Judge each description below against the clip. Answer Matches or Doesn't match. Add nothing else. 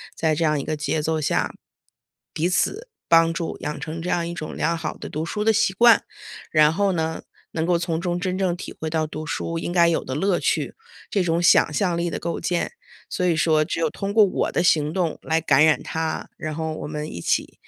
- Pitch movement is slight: Matches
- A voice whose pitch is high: Doesn't match